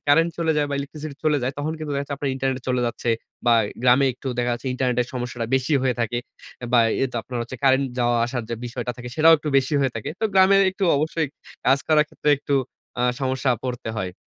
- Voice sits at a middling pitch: No, low, 130 Hz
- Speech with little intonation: No, average, 3.2 semitones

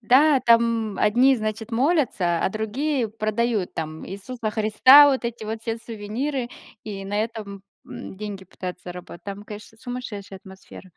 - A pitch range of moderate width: Yes, average, 3.3 semitones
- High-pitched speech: Yes, high, 220 Hz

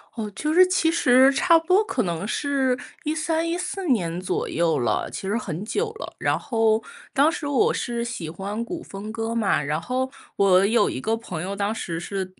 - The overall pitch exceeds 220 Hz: Yes, high, 230 Hz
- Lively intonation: Yes, wide, 7.7 semitones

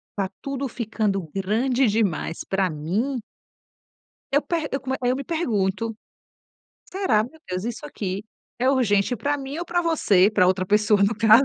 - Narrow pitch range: No, wide, 5.5 semitones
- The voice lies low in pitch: No, high, 225 Hz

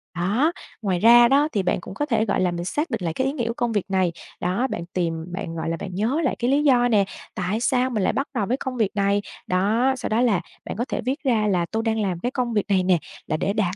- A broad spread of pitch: No, average, 5.0 semitones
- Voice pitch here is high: Yes, high, 220 Hz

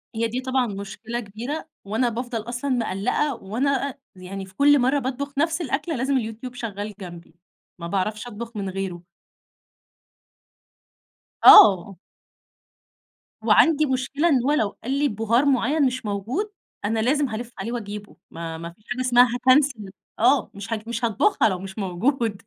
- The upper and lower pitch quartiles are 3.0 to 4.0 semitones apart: No, average, 4.5 semitones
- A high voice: Yes, high, 235 Hz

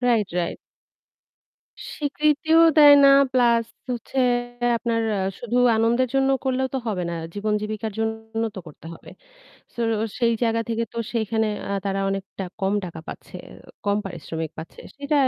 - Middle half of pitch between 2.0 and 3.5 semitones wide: No, average, 4.1 semitones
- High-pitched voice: Yes, high, 225 Hz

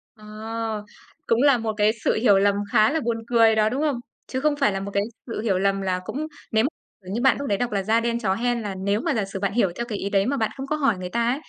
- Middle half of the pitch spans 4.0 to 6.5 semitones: No, average, 3.4 semitones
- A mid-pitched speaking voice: No, high, 220 Hz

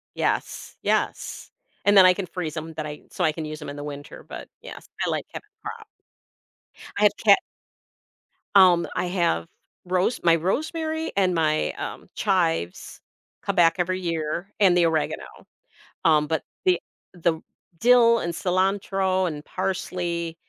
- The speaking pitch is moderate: Yes, medium, 175 Hz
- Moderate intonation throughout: Yes, average, 3.1 semitones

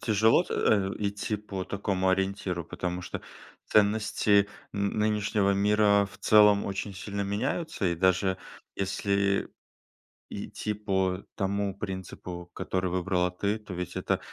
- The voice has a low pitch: Yes, low, 100 Hz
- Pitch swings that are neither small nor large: No, narrow, 1.9 semitones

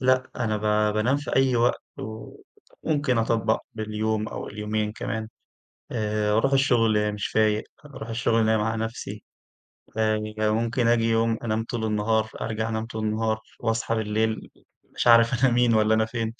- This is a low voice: Yes, low, 110 Hz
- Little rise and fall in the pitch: Yes, narrow, 1.3 semitones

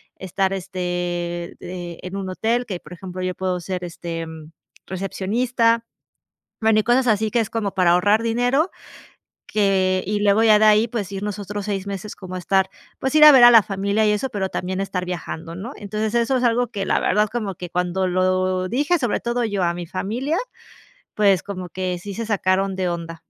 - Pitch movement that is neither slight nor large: Yes, average, 3.2 semitones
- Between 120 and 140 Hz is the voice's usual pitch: No, high, 195 Hz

